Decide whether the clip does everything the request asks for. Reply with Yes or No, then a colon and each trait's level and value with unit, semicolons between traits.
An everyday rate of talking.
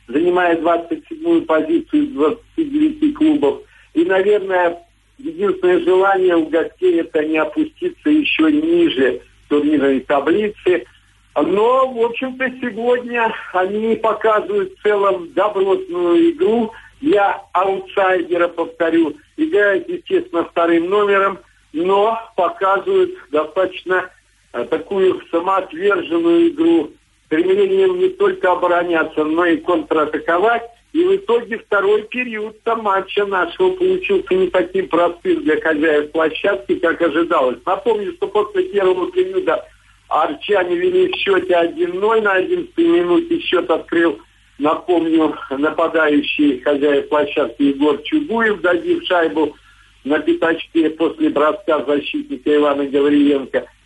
No: slow, 105 wpm